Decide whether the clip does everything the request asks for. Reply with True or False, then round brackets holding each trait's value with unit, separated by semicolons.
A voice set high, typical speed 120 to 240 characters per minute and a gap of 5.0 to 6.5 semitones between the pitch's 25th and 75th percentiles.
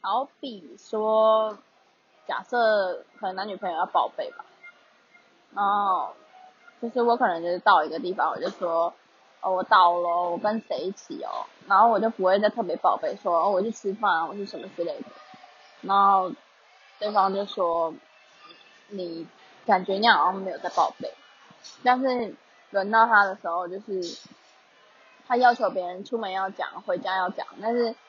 False (205 Hz; 230 characters per minute; 4.3 semitones)